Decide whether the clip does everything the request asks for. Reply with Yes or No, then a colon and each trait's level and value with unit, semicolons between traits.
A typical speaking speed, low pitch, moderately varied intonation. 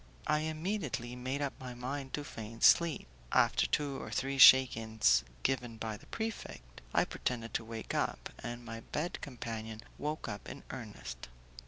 Yes: average, 160 wpm; low, 125 Hz; average, 4.2 semitones